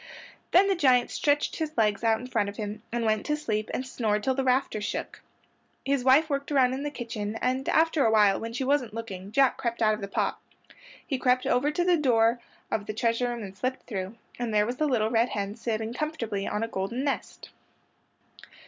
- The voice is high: Yes, high, 235 Hz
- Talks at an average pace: No, fast, 215 wpm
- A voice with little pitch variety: No, average, 3.9 semitones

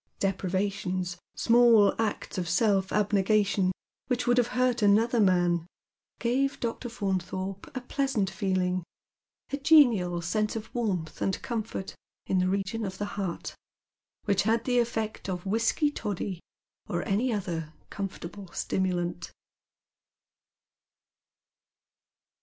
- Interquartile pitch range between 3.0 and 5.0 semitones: Yes, average, 3.8 semitones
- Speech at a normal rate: No, slow, 115 wpm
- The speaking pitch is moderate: No, high, 200 Hz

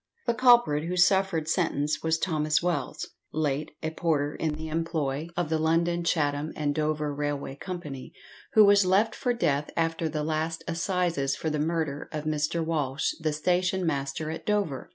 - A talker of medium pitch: Yes, medium, 160 Hz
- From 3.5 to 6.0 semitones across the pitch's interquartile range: No, narrow, 2.5 semitones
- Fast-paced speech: No, average, 170 wpm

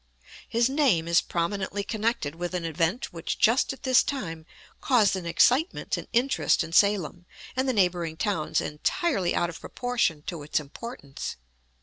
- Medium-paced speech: Yes, average, 155 wpm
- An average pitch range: No, wide, 6.4 semitones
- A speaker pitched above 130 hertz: Yes, medium, 185 Hz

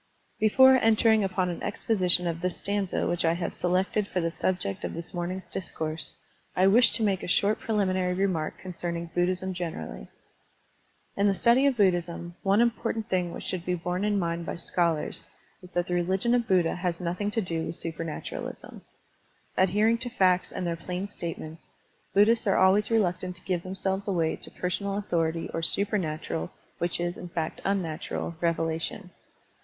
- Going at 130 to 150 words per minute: No, average, 175 wpm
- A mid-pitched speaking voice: Yes, medium, 180 Hz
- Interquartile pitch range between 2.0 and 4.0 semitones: Yes, average, 2.9 semitones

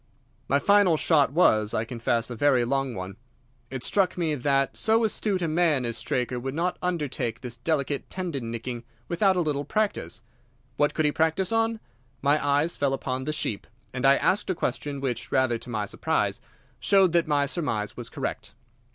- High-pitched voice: No, medium, 140 Hz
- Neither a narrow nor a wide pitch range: No, wide, 5.8 semitones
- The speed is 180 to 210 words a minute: Yes, average, 185 wpm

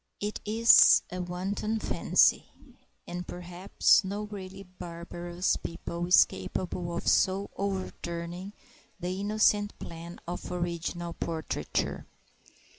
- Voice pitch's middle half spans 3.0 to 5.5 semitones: No, narrow, 2.4 semitones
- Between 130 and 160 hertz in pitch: No, medium, 180 Hz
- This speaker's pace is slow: Yes, slow, 105 wpm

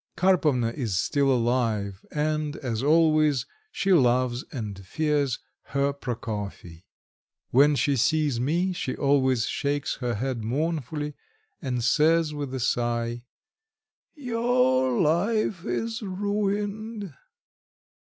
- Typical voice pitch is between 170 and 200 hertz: No, medium, 140 Hz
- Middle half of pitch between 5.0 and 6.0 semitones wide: Yes, average, 5.3 semitones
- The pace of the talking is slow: Yes, slow, 105 wpm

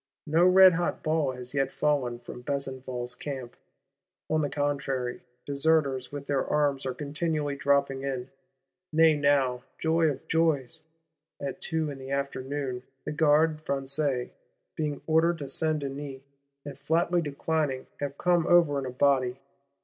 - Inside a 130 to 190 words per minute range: Yes, average, 140 wpm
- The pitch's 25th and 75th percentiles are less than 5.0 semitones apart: Yes, average, 2.9 semitones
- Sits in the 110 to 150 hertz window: Yes, medium, 140 Hz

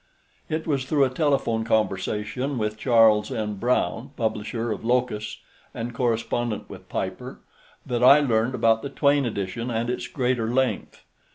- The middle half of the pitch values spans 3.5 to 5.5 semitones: No, narrow, 2.6 semitones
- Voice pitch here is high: No, low, 120 Hz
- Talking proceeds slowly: No, average, 150 wpm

